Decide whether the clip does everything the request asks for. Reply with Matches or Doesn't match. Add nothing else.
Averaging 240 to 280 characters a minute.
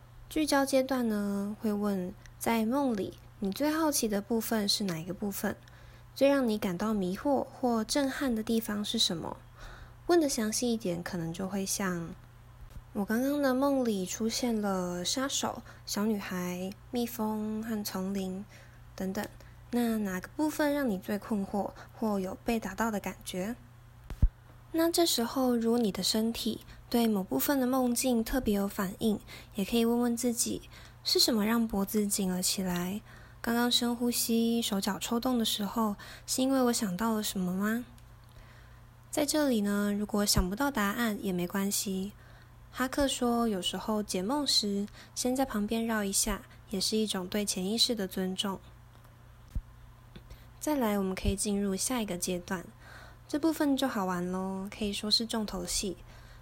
Doesn't match